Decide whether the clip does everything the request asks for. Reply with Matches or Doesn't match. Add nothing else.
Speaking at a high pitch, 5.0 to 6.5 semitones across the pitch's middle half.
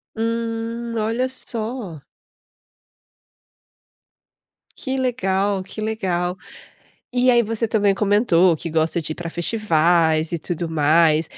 Matches